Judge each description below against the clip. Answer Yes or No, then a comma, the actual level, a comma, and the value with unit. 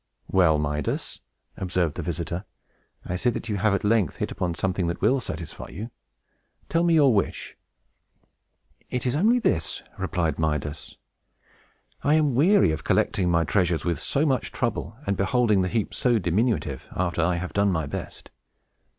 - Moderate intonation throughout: No, wide, 6.2 semitones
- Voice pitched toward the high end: No, very low, 95 Hz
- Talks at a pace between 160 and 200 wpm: Yes, average, 165 wpm